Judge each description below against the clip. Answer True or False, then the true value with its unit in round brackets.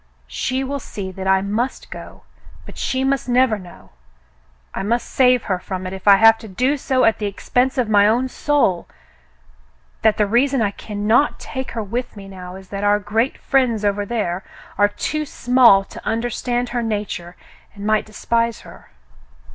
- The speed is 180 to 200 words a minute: True (185 wpm)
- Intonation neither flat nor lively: True (4.1 semitones)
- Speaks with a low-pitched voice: False (215 Hz)